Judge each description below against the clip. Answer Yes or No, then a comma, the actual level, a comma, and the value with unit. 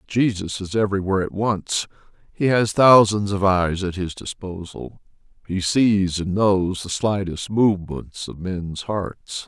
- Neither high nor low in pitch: No, very low, 95 Hz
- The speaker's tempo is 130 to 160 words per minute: Yes, average, 145 wpm